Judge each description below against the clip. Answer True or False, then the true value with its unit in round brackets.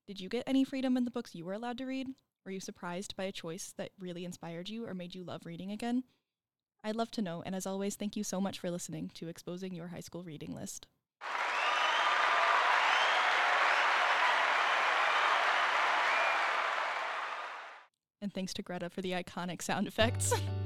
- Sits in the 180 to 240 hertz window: True (190 Hz)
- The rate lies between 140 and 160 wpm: False (170 wpm)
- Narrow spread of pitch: False (3.6 semitones)